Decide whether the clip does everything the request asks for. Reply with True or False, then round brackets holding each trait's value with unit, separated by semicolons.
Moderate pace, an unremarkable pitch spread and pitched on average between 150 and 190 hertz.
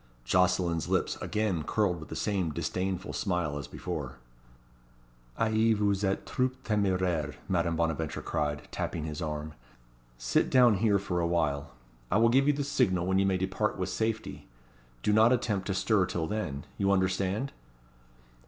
False (160 wpm; 4.2 semitones; 95 Hz)